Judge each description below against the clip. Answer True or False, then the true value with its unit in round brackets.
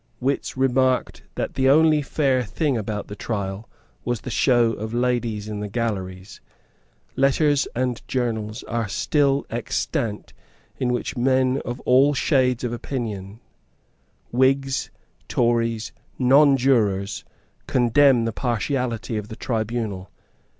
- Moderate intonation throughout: True (3.3 semitones)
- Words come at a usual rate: False (120 wpm)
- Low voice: True (120 Hz)